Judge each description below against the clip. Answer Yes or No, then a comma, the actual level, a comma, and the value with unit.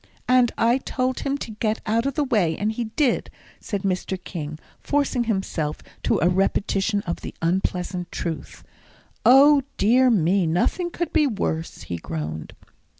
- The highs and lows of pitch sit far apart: Yes, wide, 6.3 semitones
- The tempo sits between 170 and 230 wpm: No, average, 155 wpm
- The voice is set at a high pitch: Yes, high, 210 Hz